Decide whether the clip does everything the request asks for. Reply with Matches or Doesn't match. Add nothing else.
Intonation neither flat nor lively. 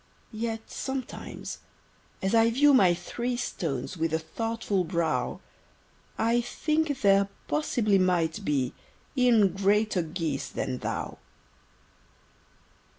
Doesn't match